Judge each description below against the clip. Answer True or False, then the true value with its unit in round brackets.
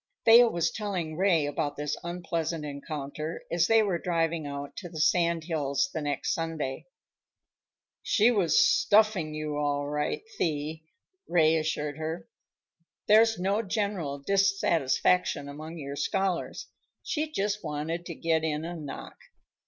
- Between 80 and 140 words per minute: True (135 wpm)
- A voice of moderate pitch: True (165 Hz)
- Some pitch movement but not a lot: True (4.0 semitones)